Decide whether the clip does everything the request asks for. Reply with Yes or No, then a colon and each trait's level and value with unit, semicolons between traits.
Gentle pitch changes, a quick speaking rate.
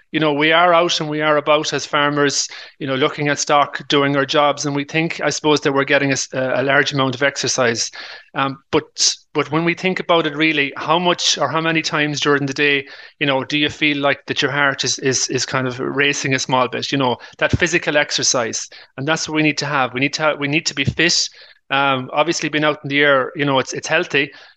Yes: narrow, 2.1 semitones; fast, 250 wpm